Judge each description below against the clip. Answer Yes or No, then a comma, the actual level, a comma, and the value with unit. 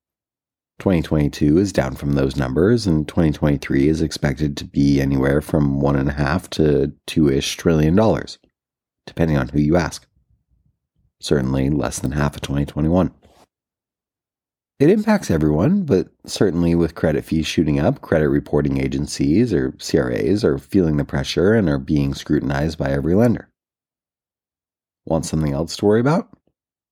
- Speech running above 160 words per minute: No, average, 145 wpm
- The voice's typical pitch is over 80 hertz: No, very low, 75 Hz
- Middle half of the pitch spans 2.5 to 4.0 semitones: Yes, average, 2.8 semitones